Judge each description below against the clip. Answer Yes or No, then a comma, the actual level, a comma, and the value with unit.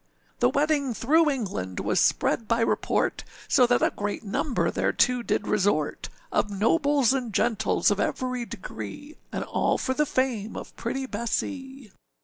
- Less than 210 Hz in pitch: No, high, 245 Hz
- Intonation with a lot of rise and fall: No, average, 4.5 semitones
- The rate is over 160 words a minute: No, average, 150 wpm